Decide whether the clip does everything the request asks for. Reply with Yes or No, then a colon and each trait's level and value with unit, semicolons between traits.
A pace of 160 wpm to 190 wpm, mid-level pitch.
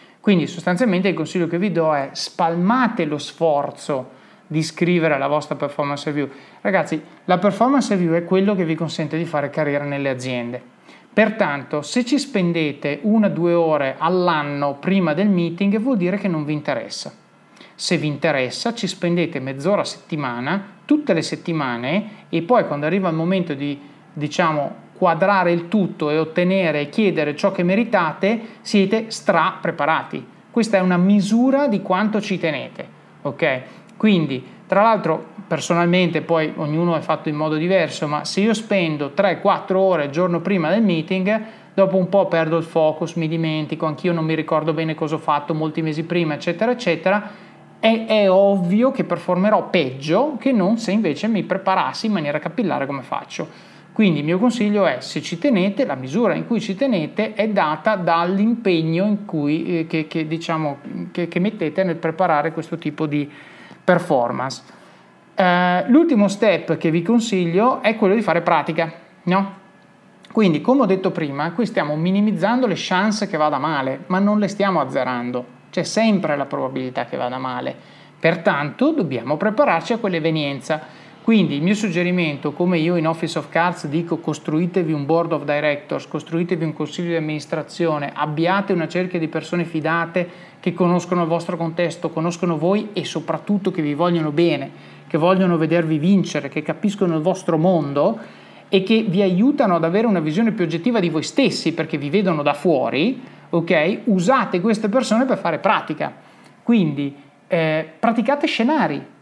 Yes: average, 165 wpm; medium, 175 Hz